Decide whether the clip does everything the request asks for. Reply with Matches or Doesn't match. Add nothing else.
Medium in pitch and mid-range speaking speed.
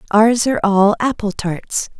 Doesn't match